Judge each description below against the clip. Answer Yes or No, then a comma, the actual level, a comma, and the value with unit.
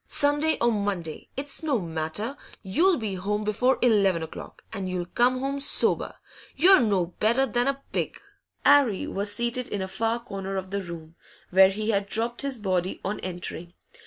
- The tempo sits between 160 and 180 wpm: Yes, average, 175 wpm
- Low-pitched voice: No, high, 210 Hz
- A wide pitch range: No, average, 5.0 semitones